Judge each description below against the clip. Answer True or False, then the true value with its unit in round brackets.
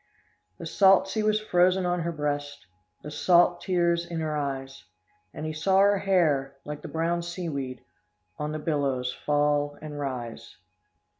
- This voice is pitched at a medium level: True (155 Hz)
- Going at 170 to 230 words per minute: False (155 wpm)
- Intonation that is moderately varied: True (3.5 semitones)